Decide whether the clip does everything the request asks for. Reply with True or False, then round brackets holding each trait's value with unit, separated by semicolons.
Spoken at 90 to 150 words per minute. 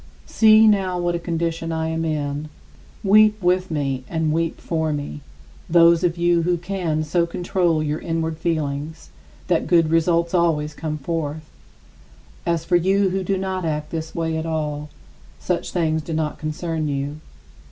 False (165 wpm)